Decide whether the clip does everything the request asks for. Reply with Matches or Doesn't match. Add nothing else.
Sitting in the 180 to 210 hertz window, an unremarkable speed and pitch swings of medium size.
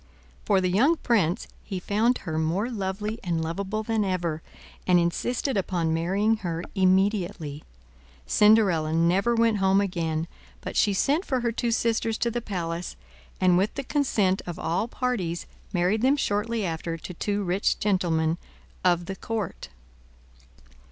Matches